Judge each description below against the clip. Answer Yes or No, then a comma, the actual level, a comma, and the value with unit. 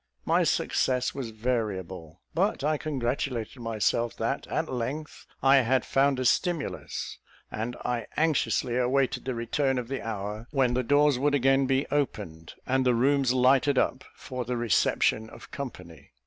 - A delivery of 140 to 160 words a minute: Yes, average, 155 wpm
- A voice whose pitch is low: Yes, low, 125 Hz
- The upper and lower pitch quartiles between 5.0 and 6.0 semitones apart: No, average, 3.0 semitones